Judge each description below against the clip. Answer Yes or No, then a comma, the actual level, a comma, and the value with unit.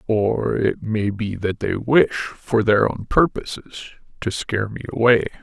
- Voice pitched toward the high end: No, low, 110 Hz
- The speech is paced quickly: No, average, 165 wpm